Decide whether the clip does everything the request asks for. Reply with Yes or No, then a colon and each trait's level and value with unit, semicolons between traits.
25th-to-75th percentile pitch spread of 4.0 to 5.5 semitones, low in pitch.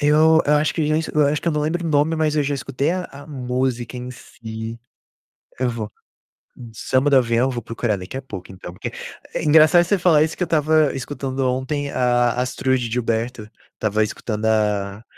Yes: average, 4.6 semitones; low, 130 Hz